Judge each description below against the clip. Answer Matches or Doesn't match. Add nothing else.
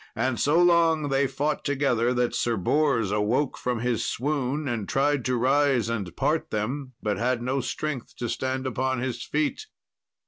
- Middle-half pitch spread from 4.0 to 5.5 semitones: Doesn't match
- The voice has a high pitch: Doesn't match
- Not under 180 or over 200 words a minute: Doesn't match